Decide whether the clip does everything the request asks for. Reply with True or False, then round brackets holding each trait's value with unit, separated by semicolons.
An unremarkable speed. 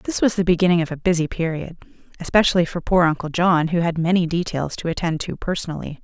False (210 wpm)